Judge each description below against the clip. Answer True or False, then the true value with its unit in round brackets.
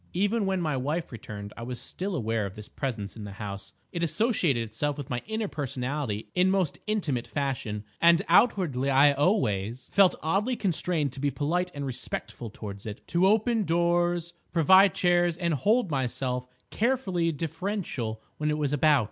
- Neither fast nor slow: True (165 wpm)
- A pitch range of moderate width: False (6.5 semitones)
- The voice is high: False (150 Hz)